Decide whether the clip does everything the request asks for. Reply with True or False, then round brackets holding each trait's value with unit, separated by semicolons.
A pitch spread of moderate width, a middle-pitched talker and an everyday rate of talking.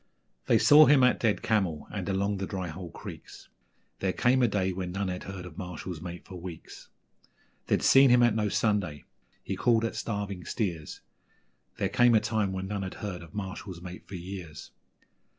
False (3.3 semitones; 95 Hz; 190 wpm)